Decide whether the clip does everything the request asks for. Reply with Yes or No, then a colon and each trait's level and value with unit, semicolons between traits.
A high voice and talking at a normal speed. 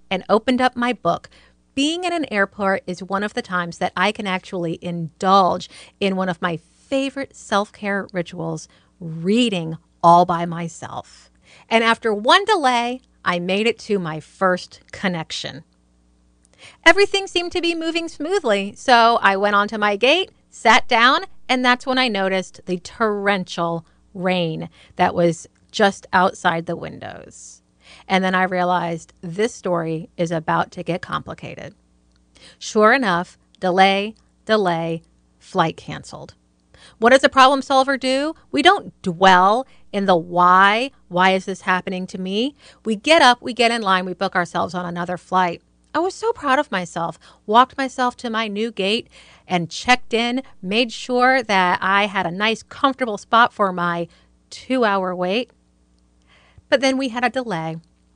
Yes: high, 195 Hz; average, 155 wpm